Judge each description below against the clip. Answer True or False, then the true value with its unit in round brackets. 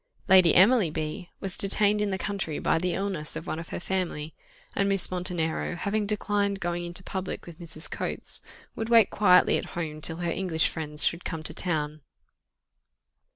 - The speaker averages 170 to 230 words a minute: True (180 wpm)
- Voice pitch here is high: False (180 Hz)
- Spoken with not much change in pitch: False (3.4 semitones)